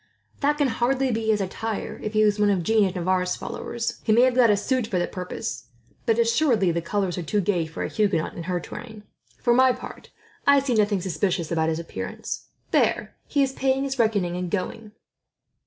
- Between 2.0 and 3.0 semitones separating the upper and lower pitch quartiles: No, average, 4.8 semitones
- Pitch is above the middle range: Yes, high, 210 Hz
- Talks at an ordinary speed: No, fast, 210 wpm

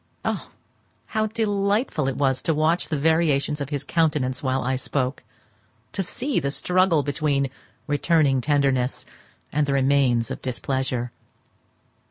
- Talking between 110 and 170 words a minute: Yes, slow, 135 wpm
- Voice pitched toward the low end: No, medium, 145 Hz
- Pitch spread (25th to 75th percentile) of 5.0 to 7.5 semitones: No, average, 3.7 semitones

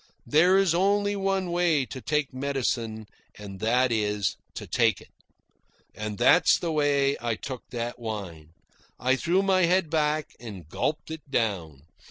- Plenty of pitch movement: Yes, wide, 7.2 semitones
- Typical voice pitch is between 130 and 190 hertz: Yes, low, 135 Hz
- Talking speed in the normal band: Yes, average, 160 wpm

